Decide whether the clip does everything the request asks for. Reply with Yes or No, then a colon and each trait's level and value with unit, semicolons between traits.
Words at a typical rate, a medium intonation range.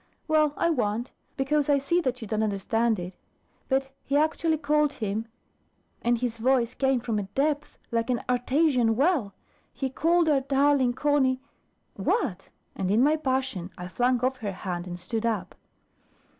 Yes: average, 170 wpm; average, 4.6 semitones